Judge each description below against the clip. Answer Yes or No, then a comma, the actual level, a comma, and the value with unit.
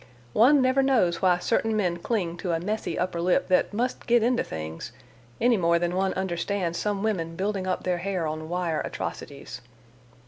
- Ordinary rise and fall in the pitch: Yes, average, 4.1 semitones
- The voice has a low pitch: No, medium, 185 Hz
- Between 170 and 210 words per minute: Yes, average, 180 wpm